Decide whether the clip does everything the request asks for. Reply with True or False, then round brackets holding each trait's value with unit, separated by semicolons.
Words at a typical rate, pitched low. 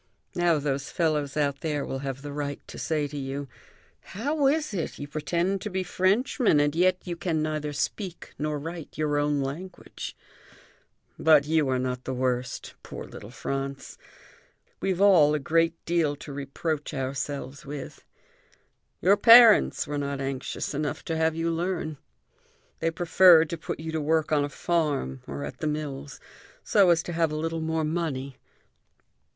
False (170 wpm; 155 Hz)